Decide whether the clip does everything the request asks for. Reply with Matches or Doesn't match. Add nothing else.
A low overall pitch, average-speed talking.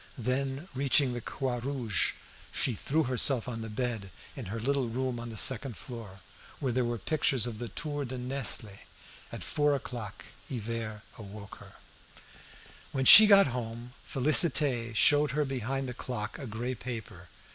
Matches